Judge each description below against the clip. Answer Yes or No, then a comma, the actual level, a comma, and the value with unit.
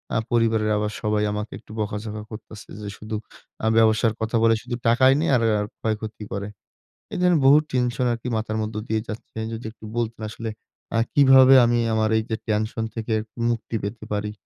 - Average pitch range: No, narrow, 1.6 semitones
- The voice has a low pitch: Yes, low, 110 Hz